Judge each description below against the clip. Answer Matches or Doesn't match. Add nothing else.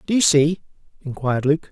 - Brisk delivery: Doesn't match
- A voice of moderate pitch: Matches